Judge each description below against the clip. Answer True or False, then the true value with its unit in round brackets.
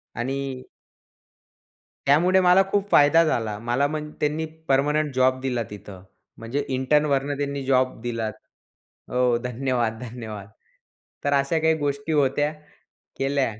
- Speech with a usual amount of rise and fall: True (3.2 semitones)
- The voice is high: False (135 Hz)